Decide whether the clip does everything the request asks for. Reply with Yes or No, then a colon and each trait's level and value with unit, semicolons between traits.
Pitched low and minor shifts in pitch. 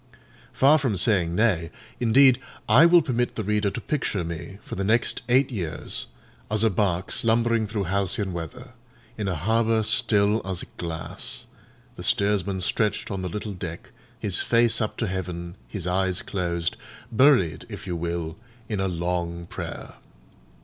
No: low, 100 Hz; average, 4.5 semitones